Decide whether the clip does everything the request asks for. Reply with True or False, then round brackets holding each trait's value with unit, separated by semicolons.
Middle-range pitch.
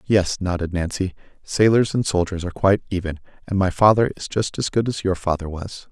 False (95 Hz)